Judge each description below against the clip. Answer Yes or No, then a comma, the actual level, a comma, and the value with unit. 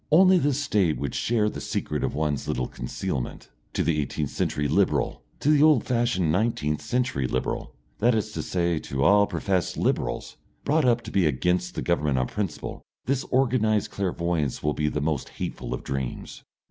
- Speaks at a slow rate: No, average, 180 wpm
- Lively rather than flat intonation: Yes, wide, 8.2 semitones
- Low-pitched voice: Yes, very low, 90 Hz